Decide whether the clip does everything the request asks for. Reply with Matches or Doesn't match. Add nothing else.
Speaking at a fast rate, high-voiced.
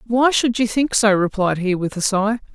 Matches